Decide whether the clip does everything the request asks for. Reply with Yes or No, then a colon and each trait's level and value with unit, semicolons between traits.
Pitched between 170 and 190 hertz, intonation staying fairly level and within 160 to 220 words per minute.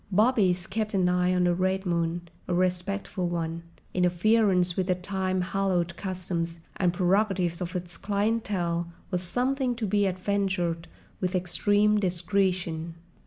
No: medium, 185 Hz; narrow, 2.3 semitones; slow, 135 wpm